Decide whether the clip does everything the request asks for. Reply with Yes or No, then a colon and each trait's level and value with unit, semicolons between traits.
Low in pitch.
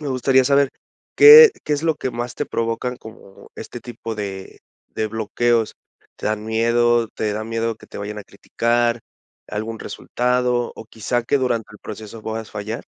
Yes: low, 115 Hz